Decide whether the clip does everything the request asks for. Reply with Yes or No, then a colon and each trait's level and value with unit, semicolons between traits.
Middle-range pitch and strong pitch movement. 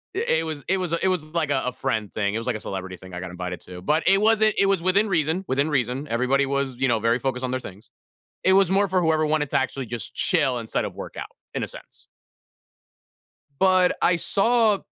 Yes: medium, 145 Hz; wide, 7.5 semitones